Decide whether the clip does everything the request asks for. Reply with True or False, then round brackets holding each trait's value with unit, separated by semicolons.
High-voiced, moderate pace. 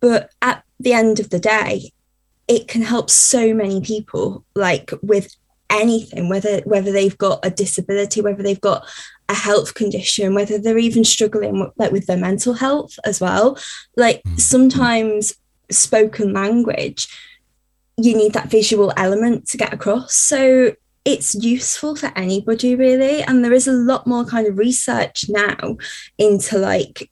True (215 Hz; 155 wpm)